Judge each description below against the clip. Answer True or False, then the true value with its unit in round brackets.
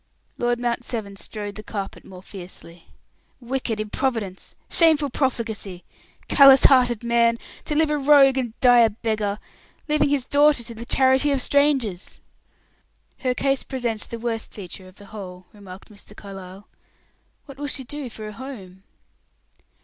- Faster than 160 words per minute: False (150 wpm)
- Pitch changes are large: False (4.7 semitones)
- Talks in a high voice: True (235 Hz)